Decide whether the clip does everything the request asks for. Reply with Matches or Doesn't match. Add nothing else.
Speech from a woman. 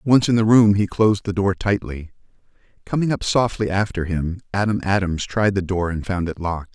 Doesn't match